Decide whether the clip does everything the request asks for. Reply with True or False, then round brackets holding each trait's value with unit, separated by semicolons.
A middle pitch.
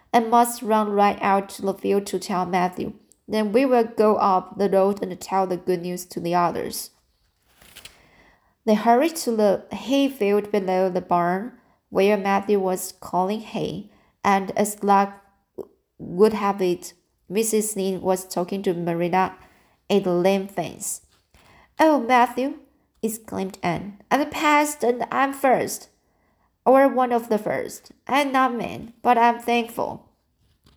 False (200 Hz)